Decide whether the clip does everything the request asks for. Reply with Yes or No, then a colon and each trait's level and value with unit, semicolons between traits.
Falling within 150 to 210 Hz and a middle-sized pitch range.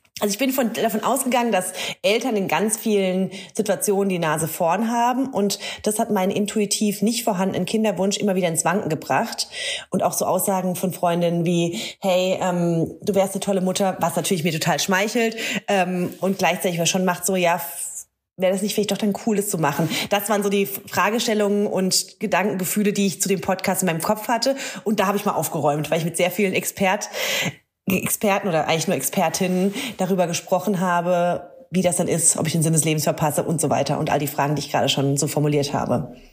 Yes: high, 190 Hz; average, 3.2 semitones